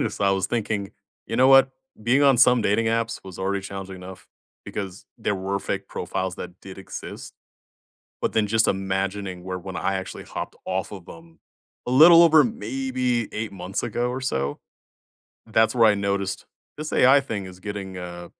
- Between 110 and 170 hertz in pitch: No, low, 100 Hz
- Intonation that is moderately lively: Yes, average, 4.2 semitones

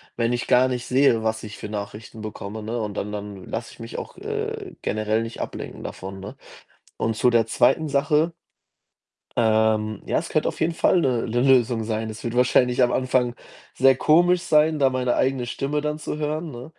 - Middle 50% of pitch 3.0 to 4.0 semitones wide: Yes, average, 3.7 semitones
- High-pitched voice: No, low, 120 Hz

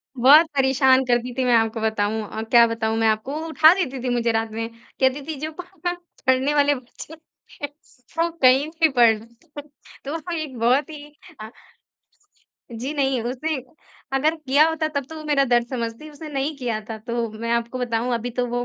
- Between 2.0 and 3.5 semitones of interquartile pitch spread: No, average, 4.3 semitones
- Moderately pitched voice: No, very high, 260 Hz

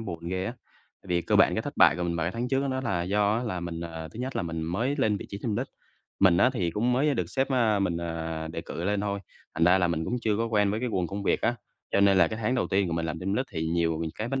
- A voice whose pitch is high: No, very low, 95 Hz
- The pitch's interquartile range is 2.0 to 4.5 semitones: No, average, 4.9 semitones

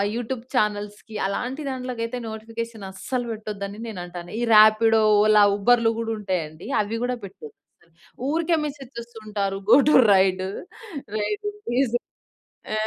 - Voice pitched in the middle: No, high, 220 Hz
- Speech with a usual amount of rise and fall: Yes, average, 3.1 semitones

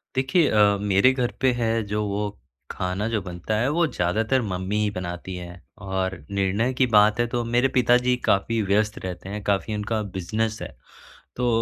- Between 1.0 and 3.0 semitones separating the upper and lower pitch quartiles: No, average, 3.7 semitones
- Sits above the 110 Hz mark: No, low, 105 Hz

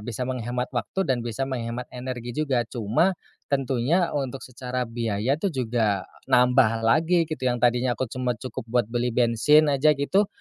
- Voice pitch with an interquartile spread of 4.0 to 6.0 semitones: No, narrow, 2.4 semitones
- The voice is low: Yes, low, 125 Hz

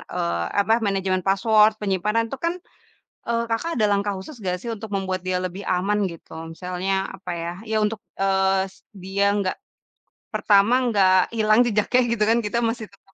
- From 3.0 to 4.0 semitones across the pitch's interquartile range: No, narrow, 2.5 semitones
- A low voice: No, high, 200 Hz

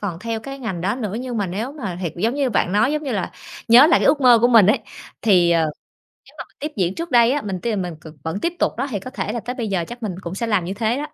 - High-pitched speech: Yes, high, 220 Hz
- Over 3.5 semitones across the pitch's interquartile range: Yes, average, 5.0 semitones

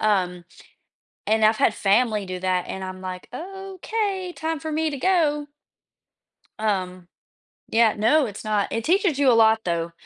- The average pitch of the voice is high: Yes, high, 220 Hz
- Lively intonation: Yes, wide, 8.8 semitones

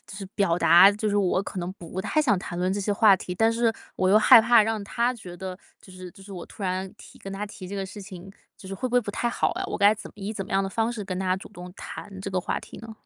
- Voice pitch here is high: Yes, high, 195 Hz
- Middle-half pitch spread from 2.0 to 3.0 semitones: Yes, narrow, 2.5 semitones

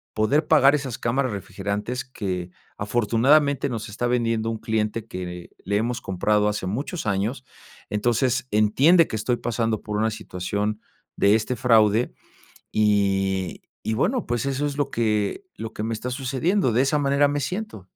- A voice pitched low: Yes, low, 115 Hz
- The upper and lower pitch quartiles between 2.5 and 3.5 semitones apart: No, average, 4.1 semitones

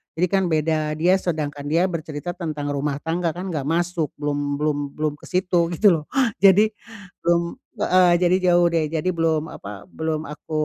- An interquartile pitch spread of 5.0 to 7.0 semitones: No, average, 2.7 semitones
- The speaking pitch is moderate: Yes, medium, 160 Hz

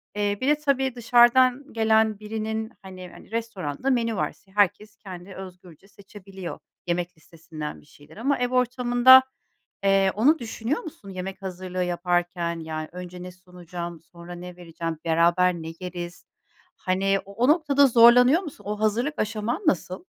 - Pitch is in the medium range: No, high, 195 Hz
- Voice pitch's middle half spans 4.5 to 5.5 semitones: Yes, average, 5.0 semitones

